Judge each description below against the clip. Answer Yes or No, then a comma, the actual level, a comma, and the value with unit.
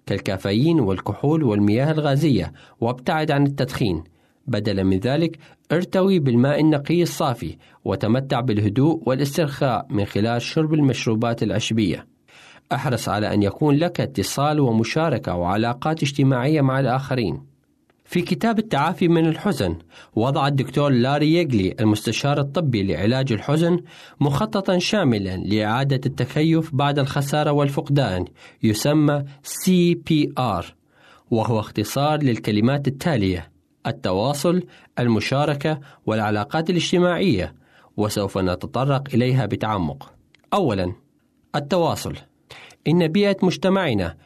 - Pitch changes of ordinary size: No, wide, 6.3 semitones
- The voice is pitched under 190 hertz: Yes, low, 135 Hz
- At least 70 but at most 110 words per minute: Yes, average, 100 wpm